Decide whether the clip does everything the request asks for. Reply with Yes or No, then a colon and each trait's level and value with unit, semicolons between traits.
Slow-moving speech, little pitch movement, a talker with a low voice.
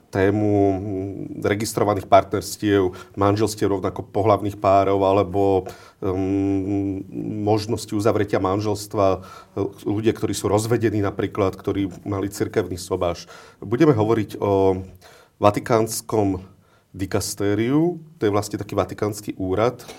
Yes: slow, 95 wpm; narrow, 1.6 semitones; low, 100 Hz